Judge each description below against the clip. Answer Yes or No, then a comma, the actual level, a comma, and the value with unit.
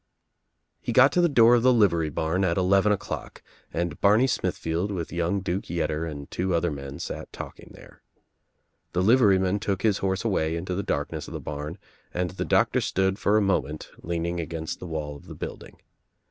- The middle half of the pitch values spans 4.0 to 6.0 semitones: No, average, 3.4 semitones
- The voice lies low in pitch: Yes, very low, 90 Hz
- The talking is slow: No, average, 190 wpm